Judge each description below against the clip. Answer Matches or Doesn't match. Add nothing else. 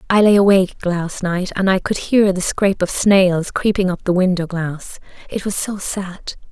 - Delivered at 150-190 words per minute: Doesn't match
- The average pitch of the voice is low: Doesn't match